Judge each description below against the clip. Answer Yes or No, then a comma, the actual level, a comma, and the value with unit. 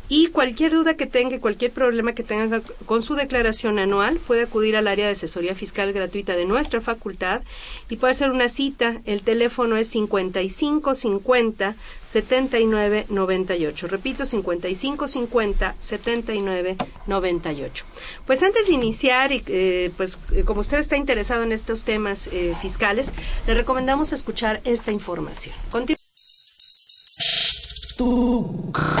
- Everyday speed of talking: No, slow, 120 wpm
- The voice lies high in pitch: Yes, high, 225 Hz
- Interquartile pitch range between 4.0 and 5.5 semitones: Yes, average, 4.4 semitones